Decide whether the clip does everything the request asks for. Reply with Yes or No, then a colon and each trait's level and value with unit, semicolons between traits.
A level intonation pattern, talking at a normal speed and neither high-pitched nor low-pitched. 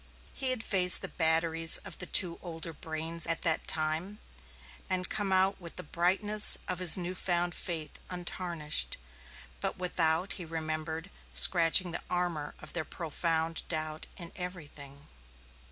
Yes: narrow, 2.2 semitones; average, 145 wpm; medium, 170 Hz